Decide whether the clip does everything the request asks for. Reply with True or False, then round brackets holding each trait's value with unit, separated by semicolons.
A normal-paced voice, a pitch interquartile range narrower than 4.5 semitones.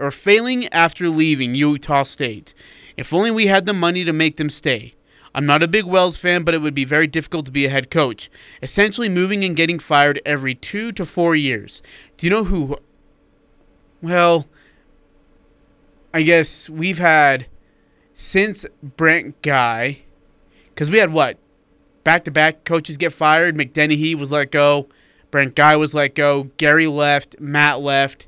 True (160 wpm; 3.0 semitones)